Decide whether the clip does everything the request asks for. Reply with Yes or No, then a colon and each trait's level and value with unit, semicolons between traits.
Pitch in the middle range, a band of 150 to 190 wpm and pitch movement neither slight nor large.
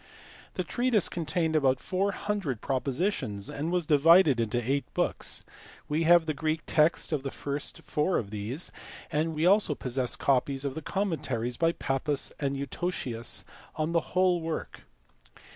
Yes: medium, 150 Hz; average, 155 wpm; average, 4.2 semitones